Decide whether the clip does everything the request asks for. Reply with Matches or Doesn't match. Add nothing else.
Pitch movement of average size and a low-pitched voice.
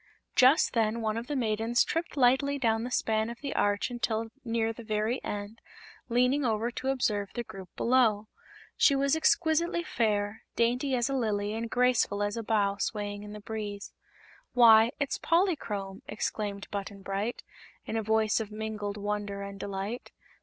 Doesn't match